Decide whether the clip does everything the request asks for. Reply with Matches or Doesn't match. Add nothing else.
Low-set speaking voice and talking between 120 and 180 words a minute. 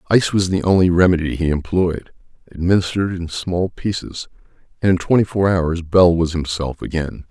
Matches